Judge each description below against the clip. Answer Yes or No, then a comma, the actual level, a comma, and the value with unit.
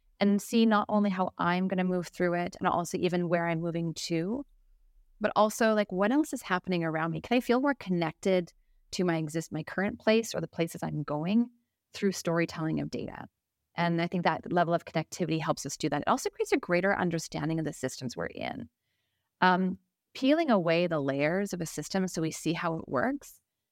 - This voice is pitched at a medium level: Yes, medium, 180 Hz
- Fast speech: Yes, fast, 210 wpm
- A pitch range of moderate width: Yes, average, 3.7 semitones